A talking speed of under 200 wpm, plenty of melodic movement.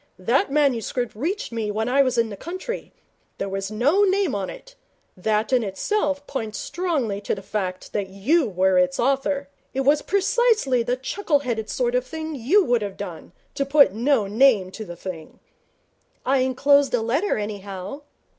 Yes: average, 175 wpm; wide, 5.7 semitones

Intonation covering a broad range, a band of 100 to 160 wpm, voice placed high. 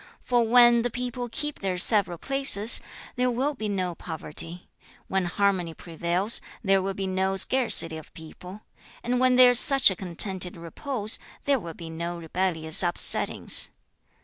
Yes: wide, 5.8 semitones; average, 155 wpm; high, 195 Hz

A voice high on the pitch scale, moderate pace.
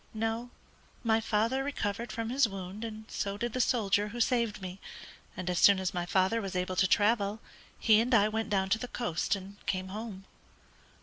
Yes: high, 210 Hz; average, 195 wpm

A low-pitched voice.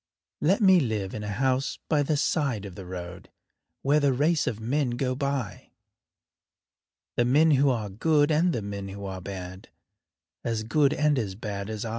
Yes: low, 125 Hz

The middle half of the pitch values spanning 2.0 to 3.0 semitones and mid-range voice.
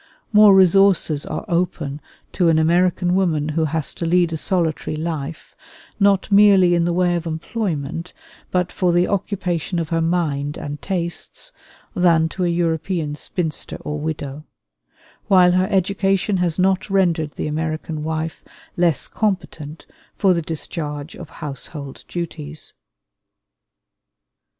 Yes: average, 2.7 semitones; medium, 170 Hz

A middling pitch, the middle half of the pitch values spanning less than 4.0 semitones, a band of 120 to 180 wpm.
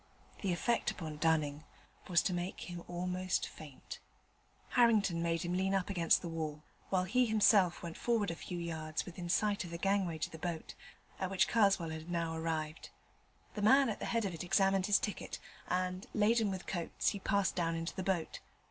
No: medium, 180 Hz; average, 3.0 semitones; average, 190 wpm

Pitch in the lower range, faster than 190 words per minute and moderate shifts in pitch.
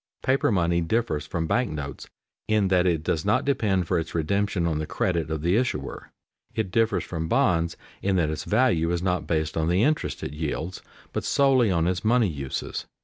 Yes: very low, 90 Hz; average, 200 wpm; average, 4.9 semitones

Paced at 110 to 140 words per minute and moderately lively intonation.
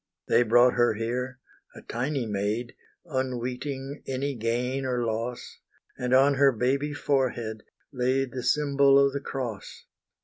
No: slow, 135 wpm; narrow, 2.3 semitones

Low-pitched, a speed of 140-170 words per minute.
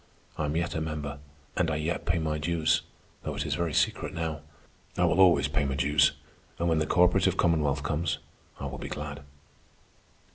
No: very low, 80 Hz; average, 190 wpm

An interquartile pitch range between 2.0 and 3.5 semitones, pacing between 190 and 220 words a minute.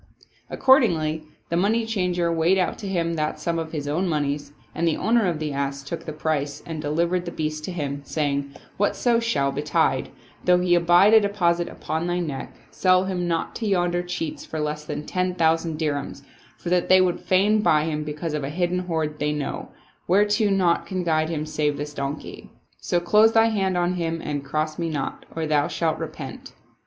Yes: average, 3.2 semitones; average, 200 wpm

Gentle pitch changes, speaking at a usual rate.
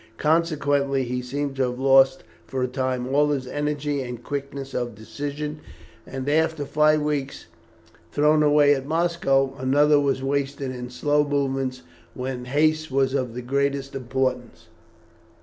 Yes: narrow, 2.1 semitones; average, 145 wpm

